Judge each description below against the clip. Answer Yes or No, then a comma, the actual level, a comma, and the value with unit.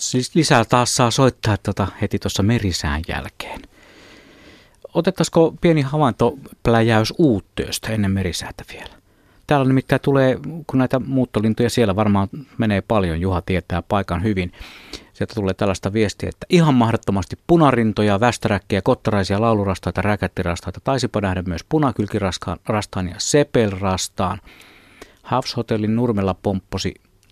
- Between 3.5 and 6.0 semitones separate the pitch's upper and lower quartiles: Yes, average, 4.6 semitones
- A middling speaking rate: Yes, average, 115 wpm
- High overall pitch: No, low, 110 Hz